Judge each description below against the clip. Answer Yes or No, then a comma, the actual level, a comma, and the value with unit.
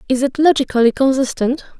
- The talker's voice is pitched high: Yes, very high, 265 Hz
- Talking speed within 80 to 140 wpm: Yes, slow, 135 wpm